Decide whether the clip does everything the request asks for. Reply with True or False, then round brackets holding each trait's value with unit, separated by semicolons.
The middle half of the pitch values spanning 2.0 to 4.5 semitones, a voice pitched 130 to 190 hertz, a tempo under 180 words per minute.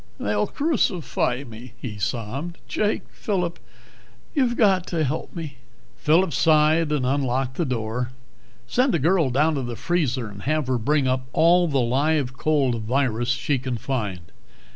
False (4.9 semitones; 135 Hz; 155 wpm)